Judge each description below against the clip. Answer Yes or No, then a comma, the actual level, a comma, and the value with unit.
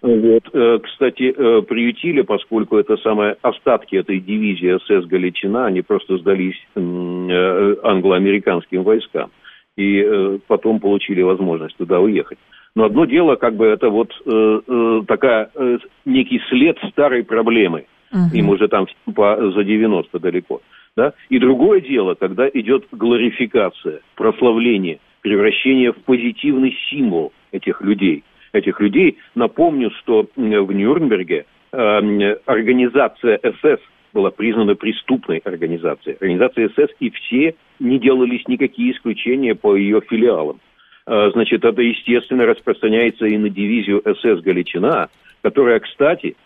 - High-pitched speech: No, low, 115 Hz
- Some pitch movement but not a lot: No, wide, 7.0 semitones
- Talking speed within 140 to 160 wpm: No, average, 115 wpm